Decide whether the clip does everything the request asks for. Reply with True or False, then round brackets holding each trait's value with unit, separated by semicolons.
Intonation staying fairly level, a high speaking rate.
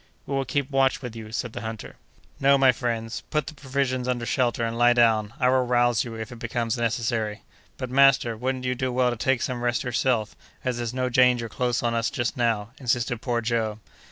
True (1.9 semitones; 215 wpm)